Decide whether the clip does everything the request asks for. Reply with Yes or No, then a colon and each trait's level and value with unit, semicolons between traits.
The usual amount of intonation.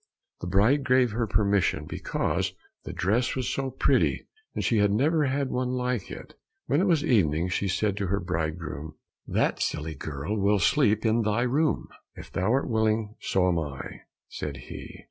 No: wide, 5.8 semitones